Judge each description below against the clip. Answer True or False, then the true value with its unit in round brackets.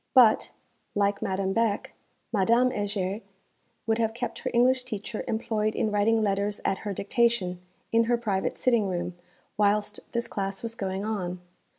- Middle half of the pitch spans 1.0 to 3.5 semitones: True (2.7 semitones)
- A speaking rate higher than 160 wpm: False (155 wpm)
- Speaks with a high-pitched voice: True (210 Hz)